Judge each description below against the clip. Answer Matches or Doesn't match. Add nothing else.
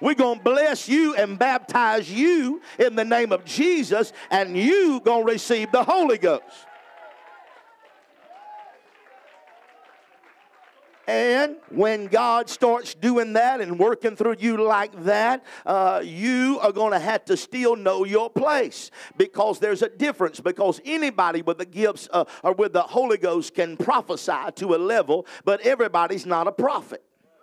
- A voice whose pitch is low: Doesn't match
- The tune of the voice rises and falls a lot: Matches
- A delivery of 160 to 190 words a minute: Doesn't match